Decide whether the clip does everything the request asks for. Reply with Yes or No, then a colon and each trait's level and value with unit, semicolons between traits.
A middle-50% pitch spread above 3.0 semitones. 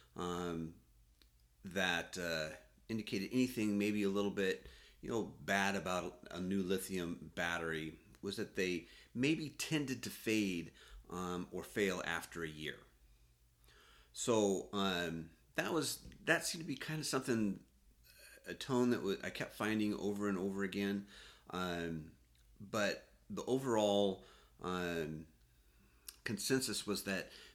Yes: average, 4.7 semitones